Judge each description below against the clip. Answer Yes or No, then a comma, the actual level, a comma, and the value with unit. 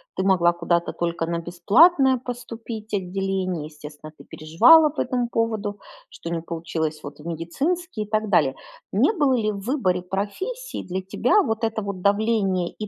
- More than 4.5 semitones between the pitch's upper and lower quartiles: Yes, wide, 5.5 semitones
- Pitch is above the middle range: Yes, high, 200 Hz